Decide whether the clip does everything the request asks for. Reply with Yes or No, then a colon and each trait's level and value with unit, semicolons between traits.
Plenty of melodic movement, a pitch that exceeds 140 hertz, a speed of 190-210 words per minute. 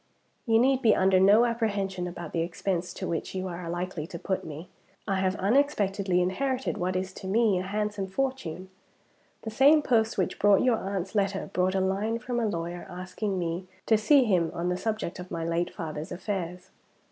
No: average, 3.5 semitones; high, 190 Hz; average, 195 wpm